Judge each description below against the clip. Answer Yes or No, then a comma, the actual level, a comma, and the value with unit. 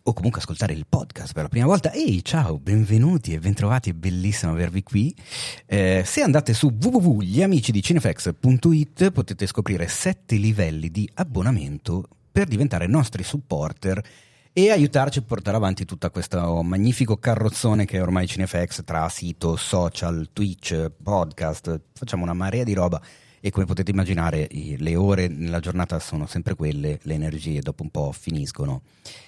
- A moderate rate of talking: Yes, average, 150 wpm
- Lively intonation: Yes, wide, 6.3 semitones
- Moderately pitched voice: No, low, 100 Hz